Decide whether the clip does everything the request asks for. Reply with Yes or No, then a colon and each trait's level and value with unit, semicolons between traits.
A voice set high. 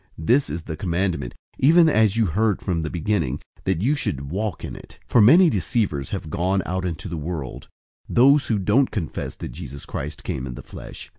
No: very low, 90 Hz